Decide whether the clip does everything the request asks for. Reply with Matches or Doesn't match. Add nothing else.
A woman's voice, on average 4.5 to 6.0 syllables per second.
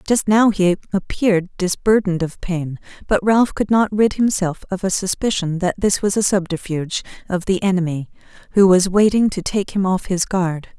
Matches